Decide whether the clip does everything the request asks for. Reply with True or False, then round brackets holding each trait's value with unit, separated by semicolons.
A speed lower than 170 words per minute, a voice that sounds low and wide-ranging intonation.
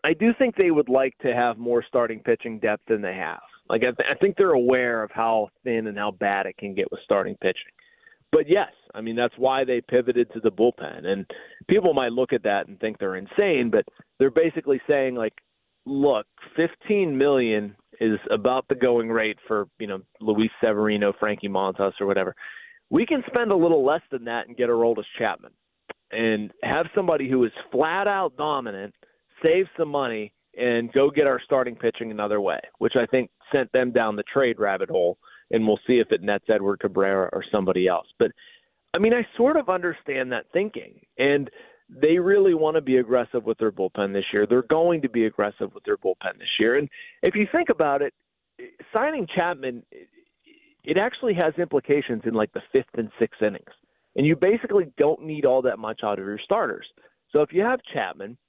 False (205 wpm; 130 Hz; 9.0 semitones)